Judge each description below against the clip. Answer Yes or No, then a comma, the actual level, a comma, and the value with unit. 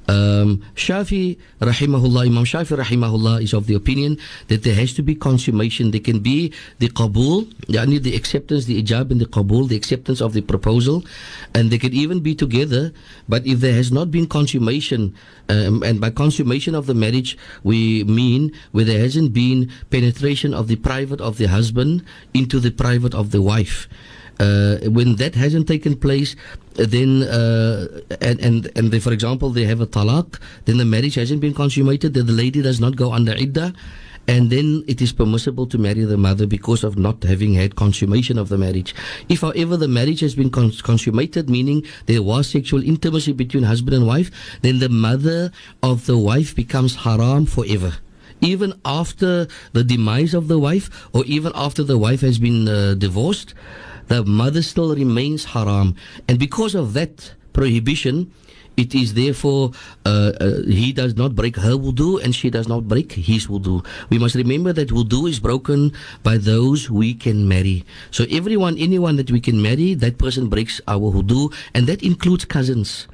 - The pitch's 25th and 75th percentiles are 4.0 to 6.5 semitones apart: Yes, average, 4.3 semitones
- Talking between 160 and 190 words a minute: Yes, average, 180 wpm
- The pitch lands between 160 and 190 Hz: No, low, 125 Hz